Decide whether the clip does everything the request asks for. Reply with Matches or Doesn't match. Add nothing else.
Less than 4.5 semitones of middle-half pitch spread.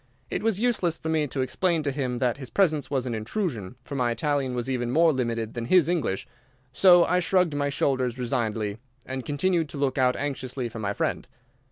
Doesn't match